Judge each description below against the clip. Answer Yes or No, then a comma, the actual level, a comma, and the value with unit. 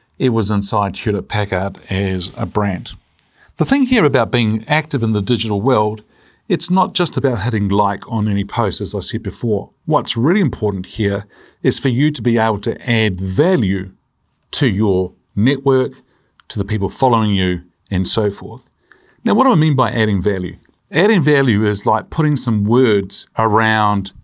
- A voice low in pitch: Yes, low, 110 Hz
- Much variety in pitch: No, average, 4.5 semitones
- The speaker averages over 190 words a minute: No, average, 175 wpm